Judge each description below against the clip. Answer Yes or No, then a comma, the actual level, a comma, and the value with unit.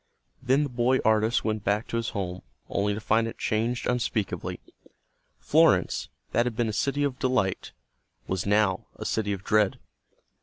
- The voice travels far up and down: No, average, 3.1 semitones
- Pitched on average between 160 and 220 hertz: No, low, 110 Hz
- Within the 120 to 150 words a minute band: No, average, 165 wpm